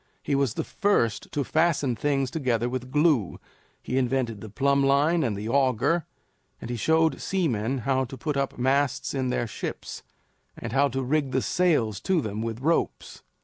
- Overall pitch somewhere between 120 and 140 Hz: Yes, low, 135 Hz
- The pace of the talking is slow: No, average, 180 wpm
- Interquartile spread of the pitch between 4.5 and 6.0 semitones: No, average, 3.6 semitones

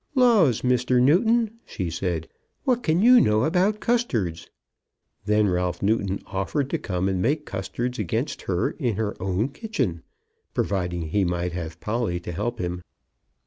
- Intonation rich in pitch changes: Yes, wide, 9.0 semitones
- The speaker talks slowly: No, average, 150 wpm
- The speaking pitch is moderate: No, low, 110 Hz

